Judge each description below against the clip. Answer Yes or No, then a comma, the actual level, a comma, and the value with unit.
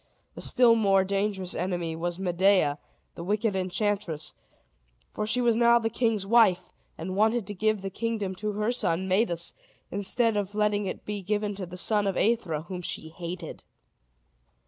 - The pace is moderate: Yes, average, 170 wpm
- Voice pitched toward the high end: Yes, high, 200 Hz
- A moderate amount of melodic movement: Yes, average, 3.1 semitones